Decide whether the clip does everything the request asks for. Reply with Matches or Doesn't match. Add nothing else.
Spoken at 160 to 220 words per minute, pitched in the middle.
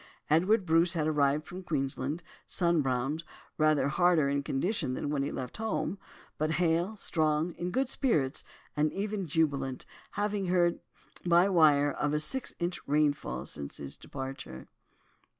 Doesn't match